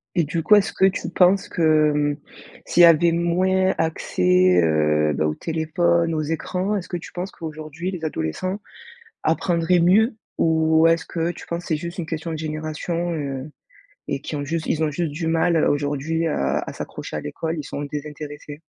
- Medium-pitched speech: Yes, medium, 160 Hz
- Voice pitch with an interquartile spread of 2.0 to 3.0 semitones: Yes, average, 2.7 semitones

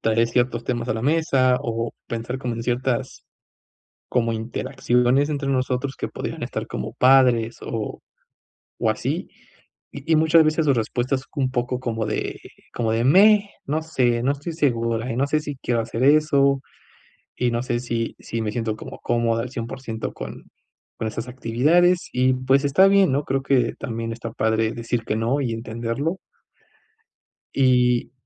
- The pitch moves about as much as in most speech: Yes, average, 3.1 semitones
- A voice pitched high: No, low, 125 Hz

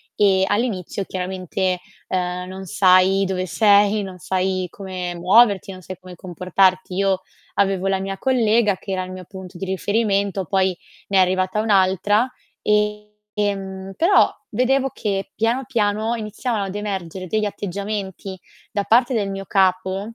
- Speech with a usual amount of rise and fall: No, narrow, 2.1 semitones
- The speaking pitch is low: No, high, 195 Hz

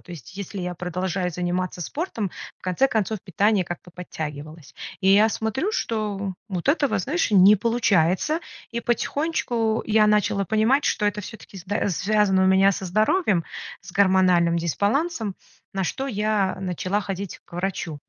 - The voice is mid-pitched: No, high, 200 Hz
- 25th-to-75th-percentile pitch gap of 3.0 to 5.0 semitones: Yes, average, 3.3 semitones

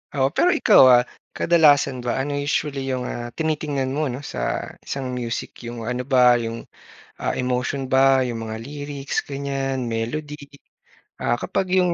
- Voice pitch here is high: No, low, 135 Hz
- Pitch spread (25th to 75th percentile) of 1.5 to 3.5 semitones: Yes, average, 2.9 semitones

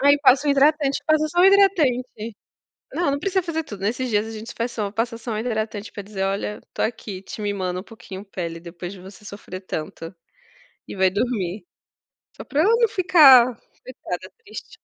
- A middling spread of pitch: No, wide, 6.3 semitones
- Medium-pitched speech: No, high, 225 Hz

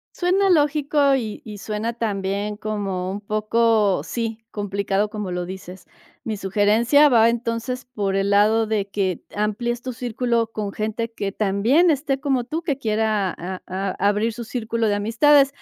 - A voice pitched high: Yes, high, 220 Hz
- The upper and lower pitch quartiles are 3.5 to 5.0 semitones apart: No, average, 3.1 semitones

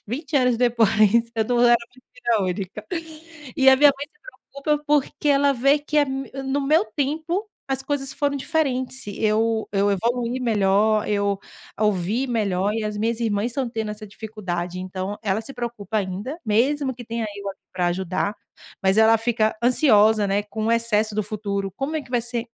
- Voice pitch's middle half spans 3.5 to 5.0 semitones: Yes, average, 4.4 semitones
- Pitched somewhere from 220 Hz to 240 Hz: Yes, high, 225 Hz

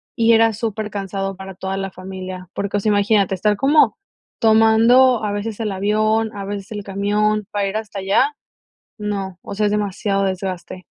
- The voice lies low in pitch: No, high, 205 Hz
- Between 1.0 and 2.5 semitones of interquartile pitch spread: Yes, narrow, 2.0 semitones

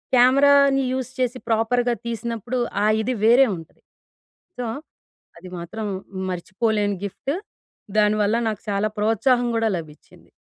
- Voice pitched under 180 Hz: No, high, 225 Hz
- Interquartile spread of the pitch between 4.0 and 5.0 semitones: No, average, 3.3 semitones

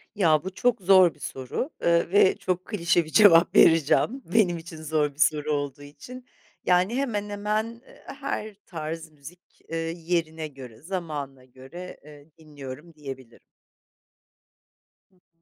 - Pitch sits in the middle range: Yes, medium, 165 Hz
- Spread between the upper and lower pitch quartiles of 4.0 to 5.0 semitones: Yes, average, 4.3 semitones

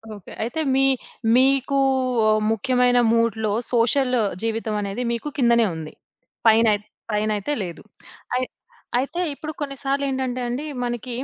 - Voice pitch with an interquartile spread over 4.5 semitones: No, average, 3.4 semitones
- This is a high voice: Yes, high, 240 Hz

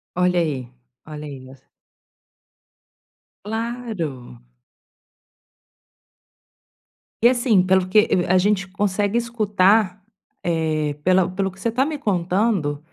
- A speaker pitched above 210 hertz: No, medium, 185 Hz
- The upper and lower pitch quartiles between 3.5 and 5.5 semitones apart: Yes, average, 5.1 semitones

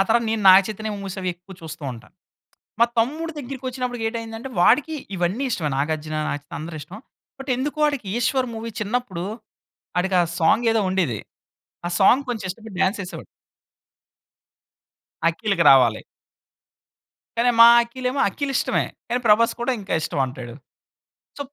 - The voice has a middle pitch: No, high, 215 Hz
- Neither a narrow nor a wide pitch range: No, wide, 6.0 semitones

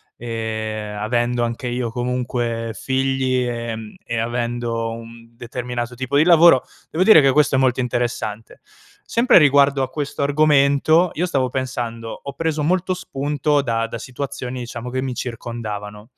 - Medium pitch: No, low, 125 Hz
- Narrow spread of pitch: No, average, 3.2 semitones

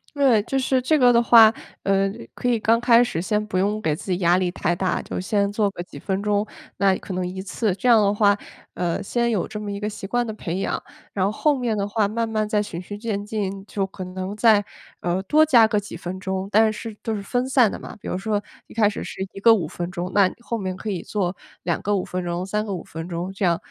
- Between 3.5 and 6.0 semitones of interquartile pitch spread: No, average, 2.9 semitones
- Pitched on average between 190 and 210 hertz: Yes, high, 205 Hz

